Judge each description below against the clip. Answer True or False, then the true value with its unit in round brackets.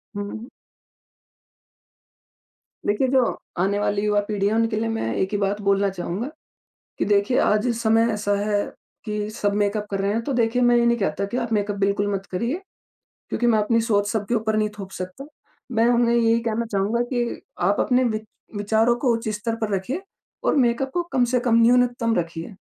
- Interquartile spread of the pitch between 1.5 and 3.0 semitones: True (2.6 semitones)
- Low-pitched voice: False (215 Hz)